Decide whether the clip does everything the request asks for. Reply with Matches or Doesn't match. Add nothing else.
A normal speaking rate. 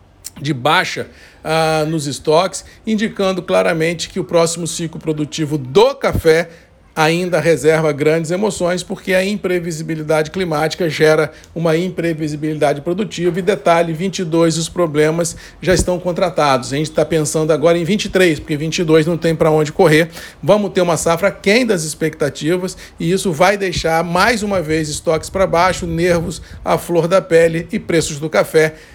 Matches